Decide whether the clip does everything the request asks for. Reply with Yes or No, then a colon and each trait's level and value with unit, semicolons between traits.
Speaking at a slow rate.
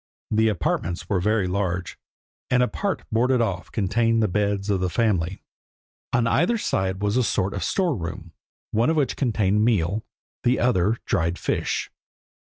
No: average, 165 wpm